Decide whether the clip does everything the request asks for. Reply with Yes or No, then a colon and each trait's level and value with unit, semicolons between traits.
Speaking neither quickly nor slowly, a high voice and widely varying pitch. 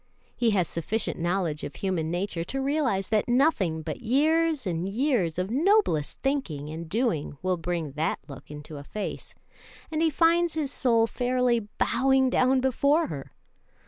Yes: average, 160 wpm; high, 220 Hz; wide, 8.2 semitones